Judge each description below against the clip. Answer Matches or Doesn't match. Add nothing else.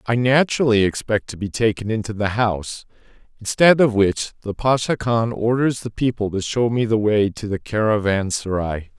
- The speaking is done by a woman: Doesn't match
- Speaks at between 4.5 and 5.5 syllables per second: Matches